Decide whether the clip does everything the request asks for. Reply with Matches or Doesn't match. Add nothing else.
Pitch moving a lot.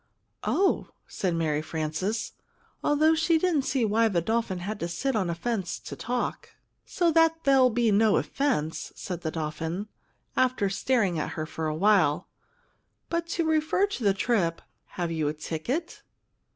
Matches